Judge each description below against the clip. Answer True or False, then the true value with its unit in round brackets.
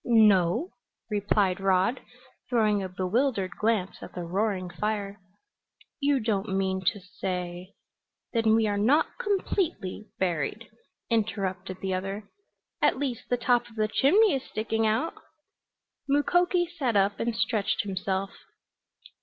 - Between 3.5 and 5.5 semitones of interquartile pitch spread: True (4.0 semitones)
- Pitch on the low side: False (210 Hz)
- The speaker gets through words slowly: True (130 wpm)